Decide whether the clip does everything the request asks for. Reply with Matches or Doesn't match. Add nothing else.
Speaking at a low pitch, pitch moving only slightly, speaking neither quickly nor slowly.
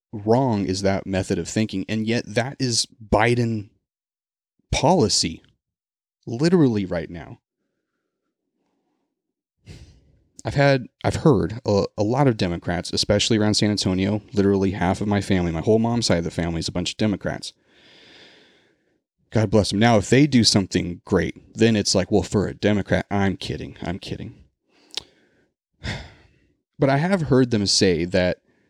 Doesn't match